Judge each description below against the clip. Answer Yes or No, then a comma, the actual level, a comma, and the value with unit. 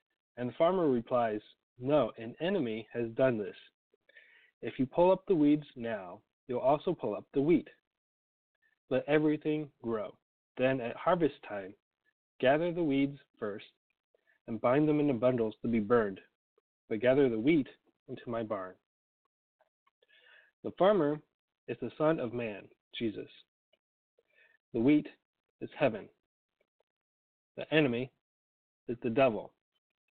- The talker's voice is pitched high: No, low, 135 Hz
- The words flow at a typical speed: No, slow, 130 wpm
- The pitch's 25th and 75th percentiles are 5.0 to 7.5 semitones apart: Yes, wide, 5.6 semitones